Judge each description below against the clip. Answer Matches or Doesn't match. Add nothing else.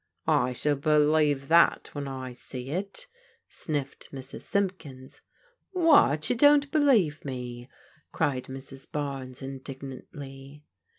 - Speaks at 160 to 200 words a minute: Doesn't match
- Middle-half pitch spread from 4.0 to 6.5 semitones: Doesn't match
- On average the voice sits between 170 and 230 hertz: Doesn't match